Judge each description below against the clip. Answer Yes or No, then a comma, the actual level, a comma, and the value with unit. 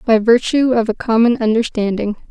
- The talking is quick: No, average, 155 wpm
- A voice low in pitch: No, high, 230 Hz